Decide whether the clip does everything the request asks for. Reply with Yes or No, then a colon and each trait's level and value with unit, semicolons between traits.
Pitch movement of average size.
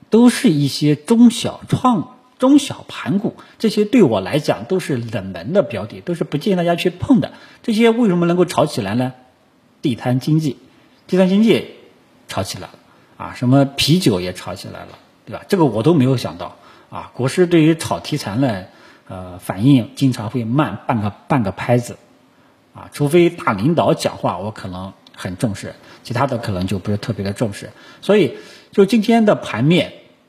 No: wide, 7.7 semitones